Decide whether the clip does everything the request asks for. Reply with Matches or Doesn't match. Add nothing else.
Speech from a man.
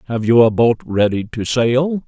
Matches